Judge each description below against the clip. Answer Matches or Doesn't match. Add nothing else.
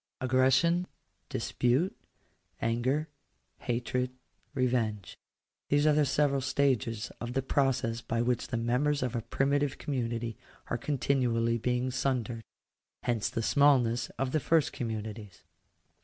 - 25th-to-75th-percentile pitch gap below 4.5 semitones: Matches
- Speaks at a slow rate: Matches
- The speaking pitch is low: Matches